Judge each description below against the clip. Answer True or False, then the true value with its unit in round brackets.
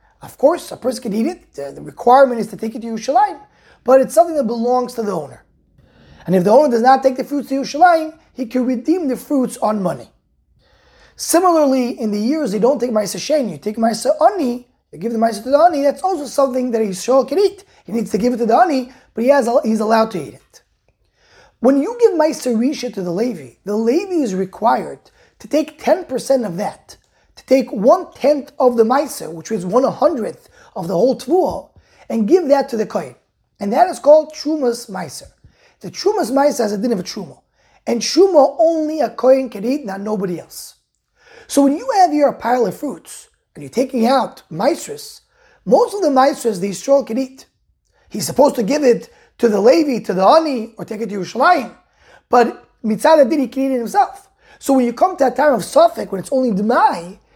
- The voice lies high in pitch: True (260 Hz)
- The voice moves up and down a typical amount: True (4.6 semitones)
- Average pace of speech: False (215 wpm)